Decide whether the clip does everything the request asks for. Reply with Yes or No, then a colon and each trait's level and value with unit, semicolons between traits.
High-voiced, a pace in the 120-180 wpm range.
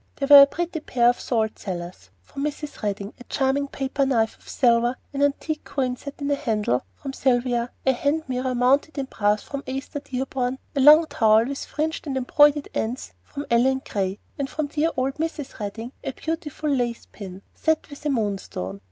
No: very high, 265 Hz; average, 195 wpm